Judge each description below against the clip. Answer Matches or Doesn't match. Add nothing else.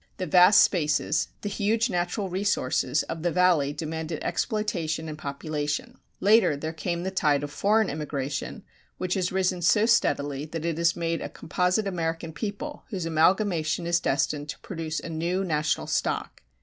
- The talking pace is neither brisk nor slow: Matches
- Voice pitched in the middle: Matches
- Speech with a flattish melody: Doesn't match